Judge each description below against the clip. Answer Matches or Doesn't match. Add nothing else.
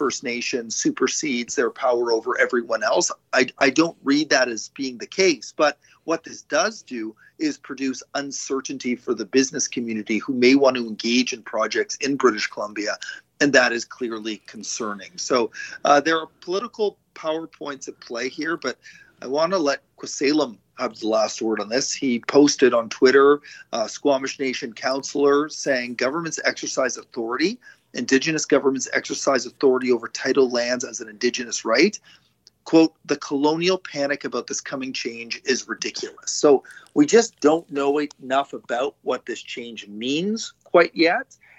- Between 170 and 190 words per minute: Doesn't match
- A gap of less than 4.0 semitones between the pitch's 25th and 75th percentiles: Doesn't match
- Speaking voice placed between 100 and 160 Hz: Matches